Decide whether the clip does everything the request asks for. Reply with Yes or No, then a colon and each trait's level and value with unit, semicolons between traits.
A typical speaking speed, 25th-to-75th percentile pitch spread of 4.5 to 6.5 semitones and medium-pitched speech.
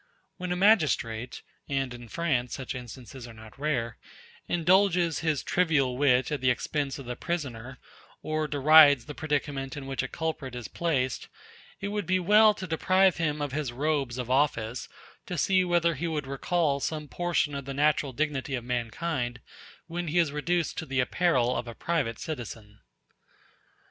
Yes: average, 170 wpm; average, 4.9 semitones; medium, 145 Hz